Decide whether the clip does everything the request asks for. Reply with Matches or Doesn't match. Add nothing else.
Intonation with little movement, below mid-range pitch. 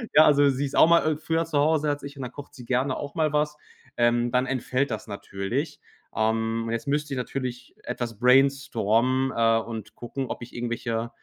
Doesn't match